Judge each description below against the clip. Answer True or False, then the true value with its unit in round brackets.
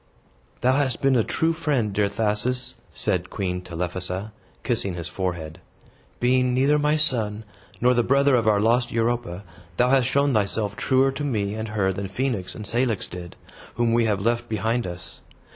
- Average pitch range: True (4.2 semitones)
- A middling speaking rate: True (175 wpm)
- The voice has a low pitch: True (115 Hz)